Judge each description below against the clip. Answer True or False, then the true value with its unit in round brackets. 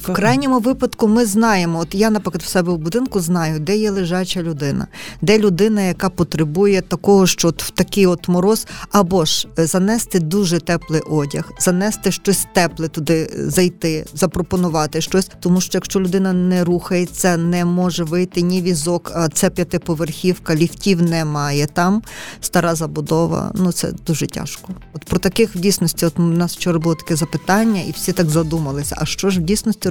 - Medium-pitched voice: True (180 Hz)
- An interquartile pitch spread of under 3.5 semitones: True (2.6 semitones)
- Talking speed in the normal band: False (170 wpm)